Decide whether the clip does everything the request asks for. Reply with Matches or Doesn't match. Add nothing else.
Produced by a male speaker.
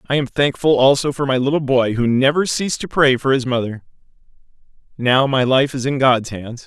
Matches